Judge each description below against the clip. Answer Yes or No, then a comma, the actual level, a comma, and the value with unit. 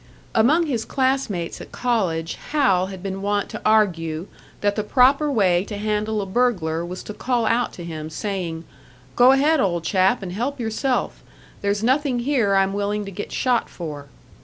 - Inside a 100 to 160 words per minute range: No, average, 180 wpm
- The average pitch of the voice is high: Yes, high, 205 Hz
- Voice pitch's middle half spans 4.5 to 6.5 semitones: Yes, average, 5.2 semitones